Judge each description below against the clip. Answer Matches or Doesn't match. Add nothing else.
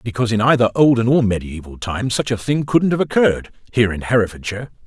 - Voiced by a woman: Doesn't match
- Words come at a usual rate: Matches